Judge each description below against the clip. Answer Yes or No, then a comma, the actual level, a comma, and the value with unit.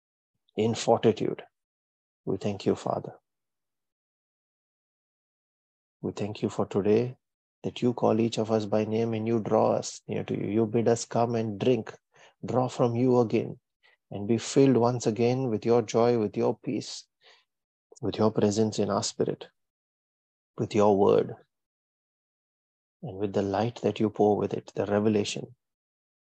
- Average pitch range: No, narrow, 2.2 semitones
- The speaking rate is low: No, average, 155 wpm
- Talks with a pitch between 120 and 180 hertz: No, low, 110 Hz